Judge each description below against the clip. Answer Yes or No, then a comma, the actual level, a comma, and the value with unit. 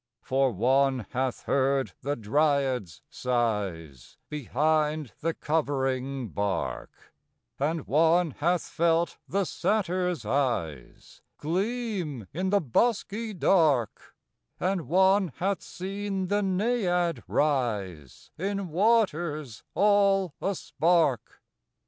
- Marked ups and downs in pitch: Yes, wide, 6.5 semitones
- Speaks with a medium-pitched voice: Yes, medium, 155 Hz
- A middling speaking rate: No, slow, 95 wpm